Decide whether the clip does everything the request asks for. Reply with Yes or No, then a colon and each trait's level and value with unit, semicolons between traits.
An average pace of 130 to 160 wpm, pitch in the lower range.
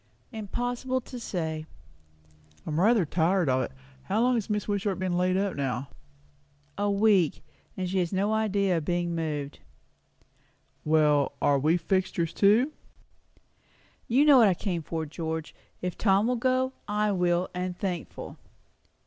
No: average, 150 wpm; medium, 185 Hz